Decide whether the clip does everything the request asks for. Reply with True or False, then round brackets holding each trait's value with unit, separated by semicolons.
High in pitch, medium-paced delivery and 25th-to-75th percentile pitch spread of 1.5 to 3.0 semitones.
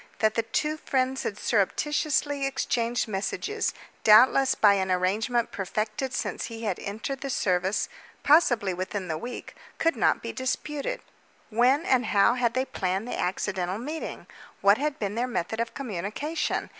False (230 Hz; 155 wpm; 5.0 semitones)